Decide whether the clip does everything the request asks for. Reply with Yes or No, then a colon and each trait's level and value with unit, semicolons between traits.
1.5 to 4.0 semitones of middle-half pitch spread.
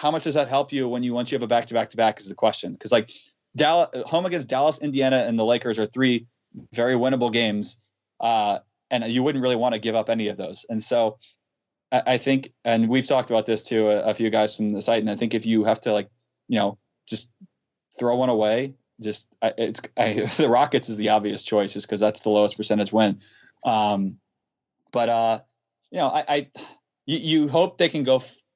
Yes: average, 3.3 semitones